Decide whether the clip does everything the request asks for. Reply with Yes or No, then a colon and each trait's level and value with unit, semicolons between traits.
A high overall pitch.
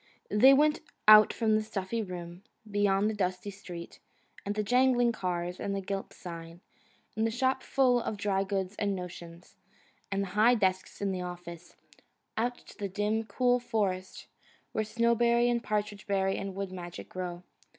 Yes: high, 200 Hz